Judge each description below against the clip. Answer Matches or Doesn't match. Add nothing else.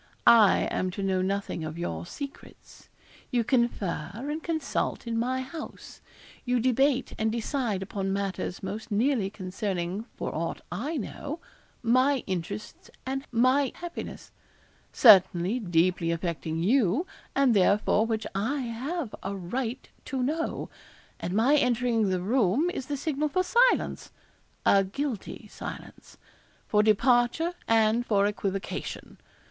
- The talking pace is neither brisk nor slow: Doesn't match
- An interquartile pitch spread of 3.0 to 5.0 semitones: Doesn't match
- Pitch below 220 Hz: Doesn't match